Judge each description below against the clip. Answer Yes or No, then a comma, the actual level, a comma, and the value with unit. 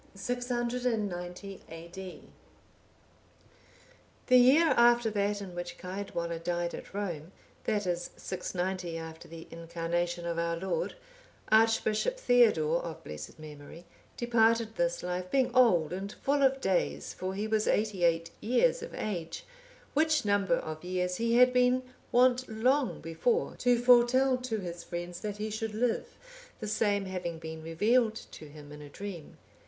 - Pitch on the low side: No, high, 200 Hz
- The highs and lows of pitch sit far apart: Yes, wide, 5.8 semitones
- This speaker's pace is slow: No, average, 145 wpm